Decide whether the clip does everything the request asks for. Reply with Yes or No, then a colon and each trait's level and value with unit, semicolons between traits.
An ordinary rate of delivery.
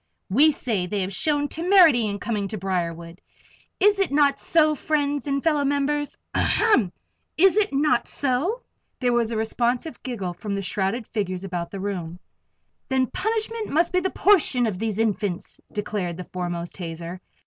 Yes: average, 165 wpm